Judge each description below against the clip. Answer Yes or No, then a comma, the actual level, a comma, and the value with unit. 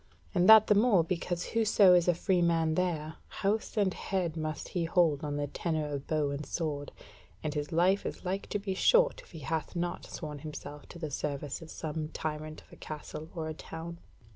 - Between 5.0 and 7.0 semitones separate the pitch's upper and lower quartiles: No, average, 3.1 semitones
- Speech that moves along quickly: Yes, fast, 210 wpm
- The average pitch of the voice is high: No, medium, 165 Hz